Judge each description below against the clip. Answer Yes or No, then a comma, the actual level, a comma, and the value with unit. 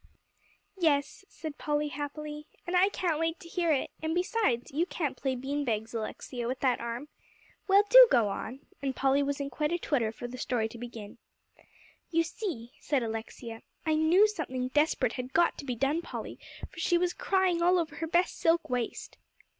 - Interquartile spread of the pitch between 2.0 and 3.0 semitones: No, average, 5.2 semitones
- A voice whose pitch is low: No, very high, 290 Hz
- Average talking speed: Yes, average, 190 wpm